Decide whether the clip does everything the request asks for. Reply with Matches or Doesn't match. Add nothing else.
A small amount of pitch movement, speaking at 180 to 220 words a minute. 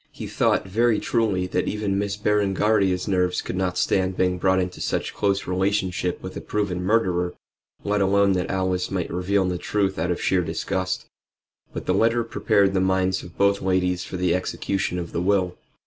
Matches